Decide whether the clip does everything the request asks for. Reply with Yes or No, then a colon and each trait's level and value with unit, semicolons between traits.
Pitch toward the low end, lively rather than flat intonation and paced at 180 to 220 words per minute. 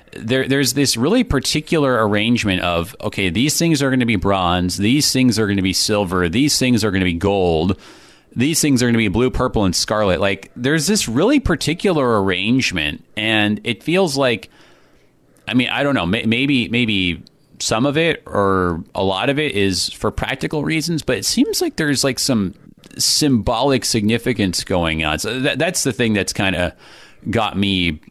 Yes: low, 115 Hz; wide, 6.5 semitones; average, 190 wpm